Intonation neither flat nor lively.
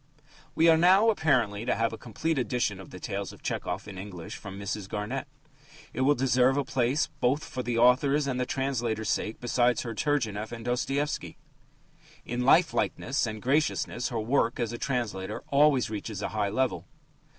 Yes: average, 4.1 semitones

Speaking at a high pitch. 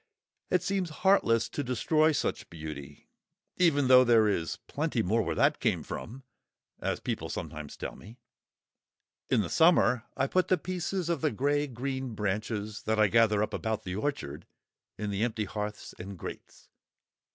No: low, 115 Hz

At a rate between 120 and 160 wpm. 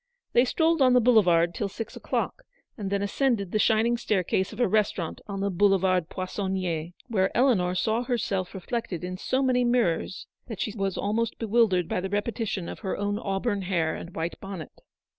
No: average, 180 wpm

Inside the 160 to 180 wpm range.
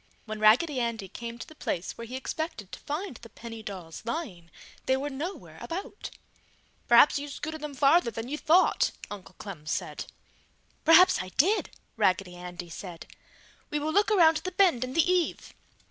Yes: average, 175 wpm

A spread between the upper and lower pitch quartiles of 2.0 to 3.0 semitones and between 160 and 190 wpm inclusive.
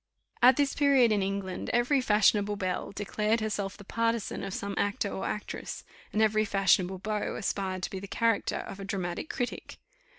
Yes: average, 2.7 semitones; average, 170 wpm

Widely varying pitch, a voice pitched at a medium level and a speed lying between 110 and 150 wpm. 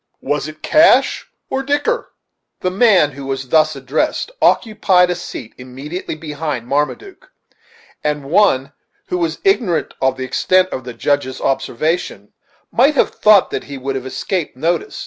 Yes: wide, 5.7 semitones; medium, 155 Hz; average, 145 wpm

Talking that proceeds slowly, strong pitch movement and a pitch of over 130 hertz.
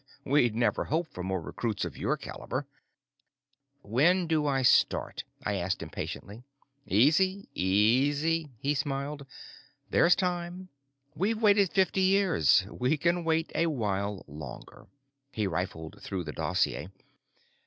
Yes: slow, 125 wpm; wide, 8.8 semitones; medium, 140 Hz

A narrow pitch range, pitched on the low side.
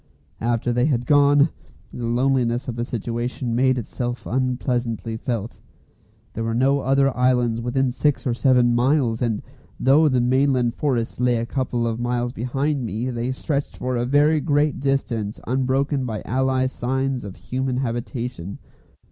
Yes: narrow, 2.1 semitones; low, 125 Hz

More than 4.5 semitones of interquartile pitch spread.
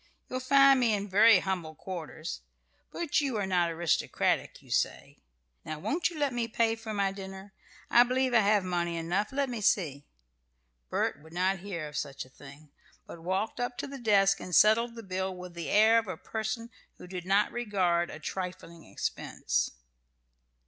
Yes: average, 4.9 semitones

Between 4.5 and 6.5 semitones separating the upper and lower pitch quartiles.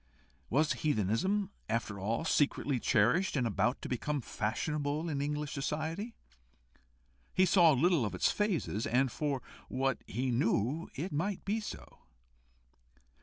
Yes: wide, 5.4 semitones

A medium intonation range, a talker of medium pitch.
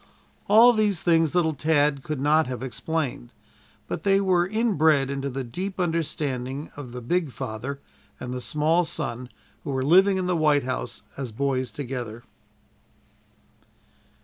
Yes: average, 5.0 semitones; medium, 145 Hz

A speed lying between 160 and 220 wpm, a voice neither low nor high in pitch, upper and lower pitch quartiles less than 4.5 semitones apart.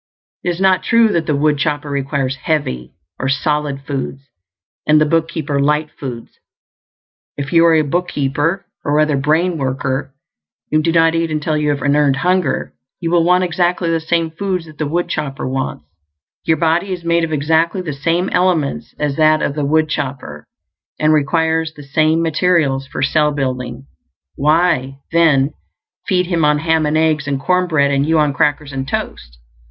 Yes: average, 175 wpm; medium, 155 Hz; average, 2.9 semitones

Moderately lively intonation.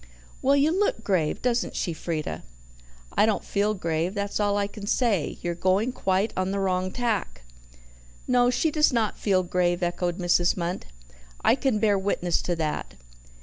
Yes: average, 4.2 semitones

